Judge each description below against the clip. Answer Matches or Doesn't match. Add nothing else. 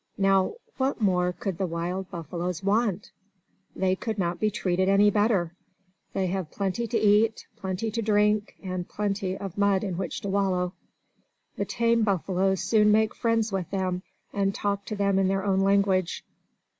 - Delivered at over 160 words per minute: Matches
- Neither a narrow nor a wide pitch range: Doesn't match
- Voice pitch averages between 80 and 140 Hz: Doesn't match